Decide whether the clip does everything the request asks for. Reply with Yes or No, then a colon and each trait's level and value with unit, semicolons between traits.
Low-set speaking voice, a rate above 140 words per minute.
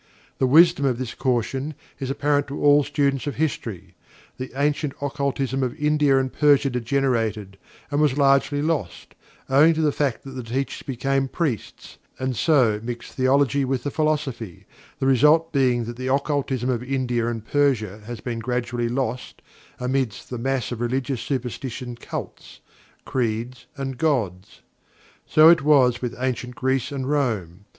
Yes: low, 130 Hz; average, 155 wpm